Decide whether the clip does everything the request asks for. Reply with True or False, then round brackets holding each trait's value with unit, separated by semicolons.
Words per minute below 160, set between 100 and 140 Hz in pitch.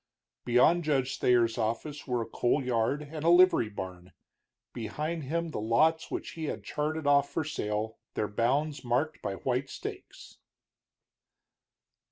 True (145 wpm; 135 Hz)